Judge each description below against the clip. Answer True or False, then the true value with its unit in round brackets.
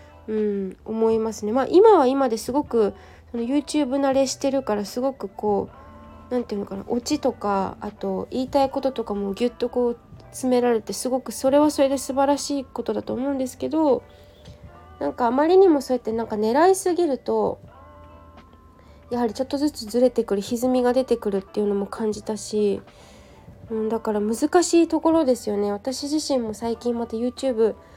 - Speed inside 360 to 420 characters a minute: True (385 characters per minute)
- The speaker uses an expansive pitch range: False (4.6 semitones)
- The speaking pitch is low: False (235 Hz)